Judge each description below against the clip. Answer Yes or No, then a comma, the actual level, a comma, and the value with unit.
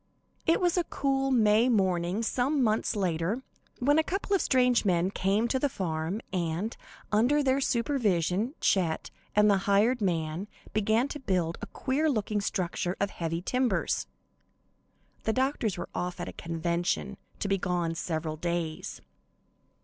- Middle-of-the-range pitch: No, high, 205 Hz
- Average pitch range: No, wide, 6.4 semitones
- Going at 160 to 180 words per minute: No, average, 150 wpm